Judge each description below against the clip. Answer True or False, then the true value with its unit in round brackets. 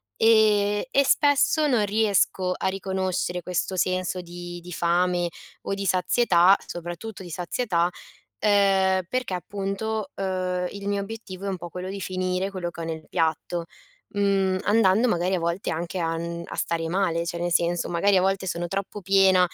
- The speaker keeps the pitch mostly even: True (2.3 semitones)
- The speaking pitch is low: False (185 Hz)